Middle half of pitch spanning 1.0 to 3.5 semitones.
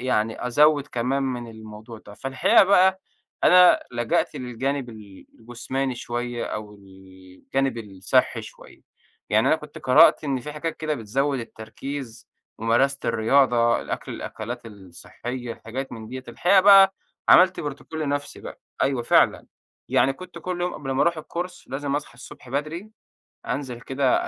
No: average, 4.1 semitones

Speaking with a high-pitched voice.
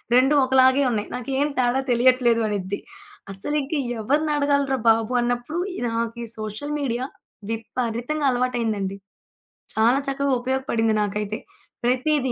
Yes: high, 245 Hz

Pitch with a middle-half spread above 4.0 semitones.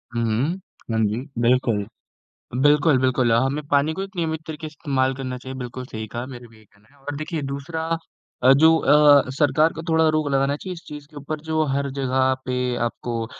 No: average, 3.3 semitones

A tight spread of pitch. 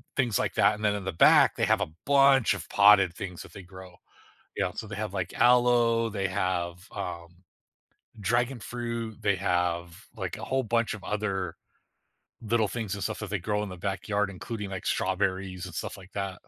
No: average, 3.3 semitones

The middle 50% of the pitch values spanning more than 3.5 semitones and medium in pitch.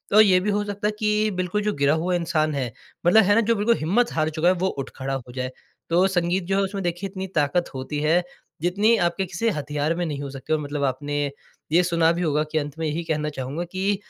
Yes: average, 4.5 semitones; medium, 170 Hz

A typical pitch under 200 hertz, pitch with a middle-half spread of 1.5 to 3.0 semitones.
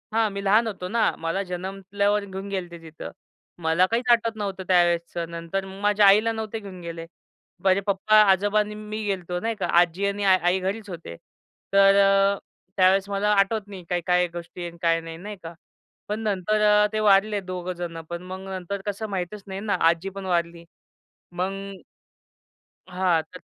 Yes: high, 190 Hz; average, 2.7 semitones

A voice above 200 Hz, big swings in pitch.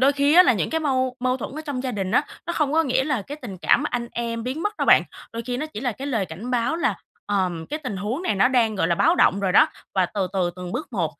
Yes: very high, 250 Hz; wide, 6.0 semitones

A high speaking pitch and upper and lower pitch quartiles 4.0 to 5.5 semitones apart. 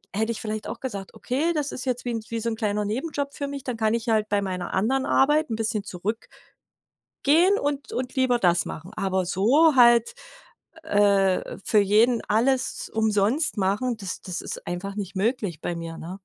Yes: high, 220 Hz; average, 4.7 semitones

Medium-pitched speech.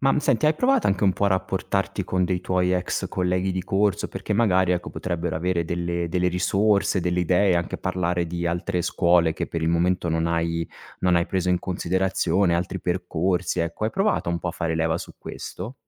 No: very low, 90 Hz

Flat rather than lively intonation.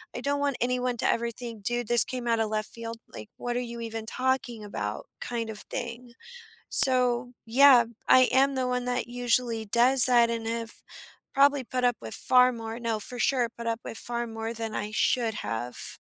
Yes: narrow, 1.8 semitones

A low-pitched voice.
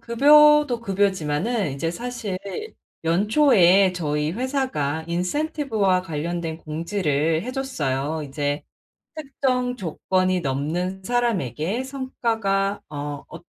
No: high, 190 Hz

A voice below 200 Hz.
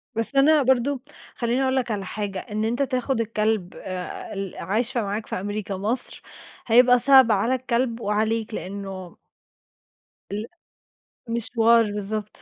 No: high, 225 Hz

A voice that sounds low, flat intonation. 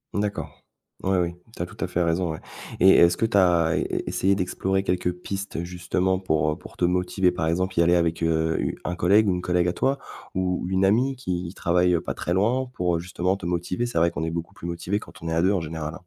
Yes: very low, 90 Hz; narrow, 2.0 semitones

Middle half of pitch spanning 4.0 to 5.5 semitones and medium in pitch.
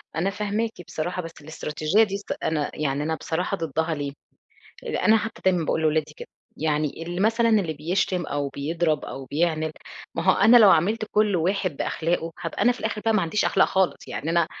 Yes: average, 4.3 semitones; medium, 170 Hz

